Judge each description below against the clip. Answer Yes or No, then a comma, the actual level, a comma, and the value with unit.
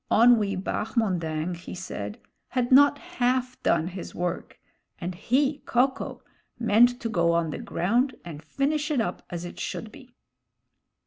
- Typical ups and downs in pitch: No, wide, 6.6 semitones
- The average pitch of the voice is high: Yes, high, 220 Hz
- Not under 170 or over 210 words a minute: No, average, 150 wpm